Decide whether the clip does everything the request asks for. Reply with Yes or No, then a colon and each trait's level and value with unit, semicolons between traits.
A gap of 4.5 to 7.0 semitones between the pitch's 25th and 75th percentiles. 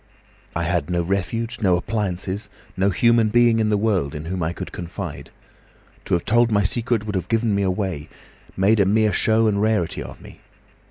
No: average, 3.9 semitones